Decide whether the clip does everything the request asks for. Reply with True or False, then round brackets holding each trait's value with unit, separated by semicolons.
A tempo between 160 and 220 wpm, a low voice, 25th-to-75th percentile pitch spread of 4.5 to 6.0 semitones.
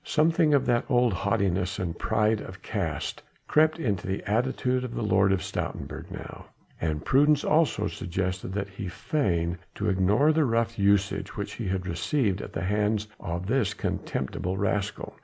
True (170 wpm; 100 Hz; 5.0 semitones)